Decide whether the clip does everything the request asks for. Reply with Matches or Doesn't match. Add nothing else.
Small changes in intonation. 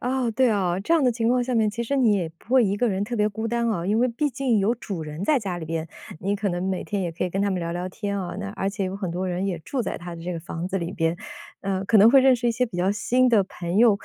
Doesn't match